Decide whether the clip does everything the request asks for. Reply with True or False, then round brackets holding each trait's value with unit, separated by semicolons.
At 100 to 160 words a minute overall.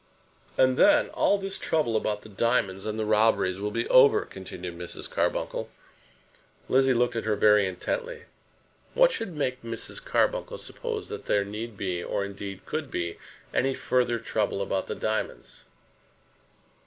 True (155 wpm)